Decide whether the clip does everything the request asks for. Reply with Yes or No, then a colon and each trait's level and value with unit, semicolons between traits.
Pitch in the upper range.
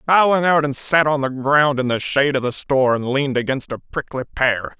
No: medium, 140 Hz